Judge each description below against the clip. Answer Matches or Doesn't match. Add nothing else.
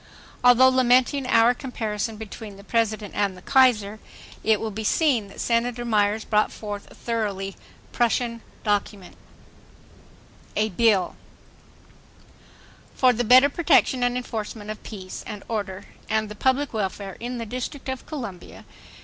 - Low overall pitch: Doesn't match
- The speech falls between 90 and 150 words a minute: Matches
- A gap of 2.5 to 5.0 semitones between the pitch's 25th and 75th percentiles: Matches